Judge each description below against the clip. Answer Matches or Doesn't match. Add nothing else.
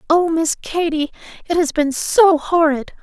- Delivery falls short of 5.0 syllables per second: Matches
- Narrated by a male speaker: Doesn't match